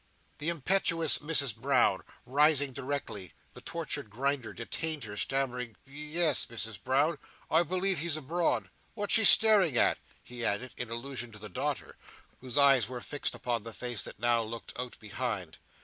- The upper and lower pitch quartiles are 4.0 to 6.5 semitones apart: Yes, average, 4.7 semitones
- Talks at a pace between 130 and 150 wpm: No, average, 165 wpm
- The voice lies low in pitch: Yes, low, 130 Hz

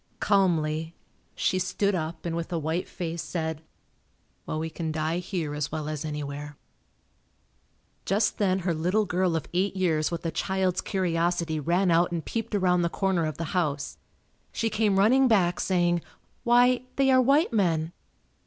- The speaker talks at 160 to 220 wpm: Yes, average, 165 wpm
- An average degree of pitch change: Yes, average, 3.2 semitones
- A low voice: No, medium, 175 Hz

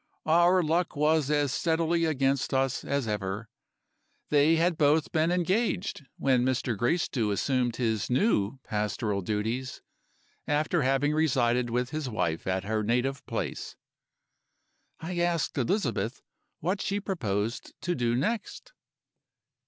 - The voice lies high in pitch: No, low, 135 Hz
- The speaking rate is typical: No, slow, 125 wpm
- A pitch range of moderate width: No, wide, 5.8 semitones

